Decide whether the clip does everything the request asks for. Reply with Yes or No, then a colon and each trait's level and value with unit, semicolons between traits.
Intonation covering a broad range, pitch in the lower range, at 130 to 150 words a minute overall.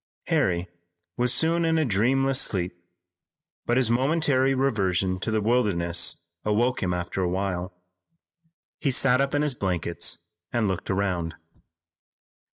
Yes: wide, 6.2 semitones; low, 110 Hz; slow, 135 wpm